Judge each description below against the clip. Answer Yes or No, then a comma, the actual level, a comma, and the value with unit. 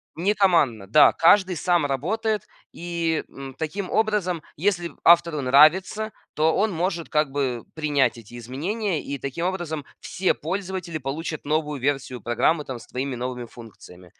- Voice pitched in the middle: Yes, medium, 155 Hz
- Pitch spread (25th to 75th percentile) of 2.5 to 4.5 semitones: No, average, 5.1 semitones